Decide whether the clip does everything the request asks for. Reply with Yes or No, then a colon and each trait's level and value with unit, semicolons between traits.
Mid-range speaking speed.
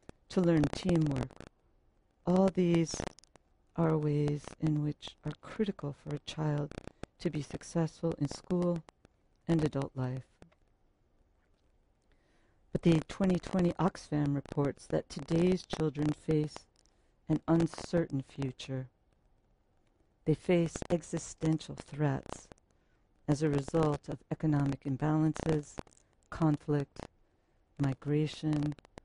No: slow, 95 wpm